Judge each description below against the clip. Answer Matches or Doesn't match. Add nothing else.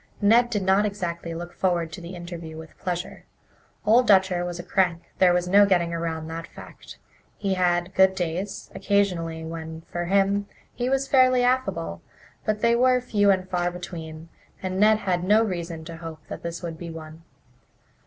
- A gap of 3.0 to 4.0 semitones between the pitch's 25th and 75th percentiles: Matches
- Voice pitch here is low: Doesn't match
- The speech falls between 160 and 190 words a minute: Matches